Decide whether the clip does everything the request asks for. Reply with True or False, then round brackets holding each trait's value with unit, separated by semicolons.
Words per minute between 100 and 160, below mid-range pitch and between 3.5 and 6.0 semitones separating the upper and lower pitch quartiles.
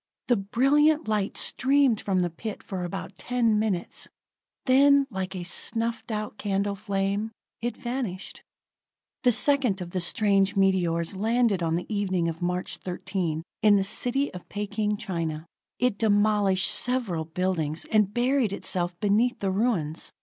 False (145 wpm; 200 Hz; 4.1 semitones)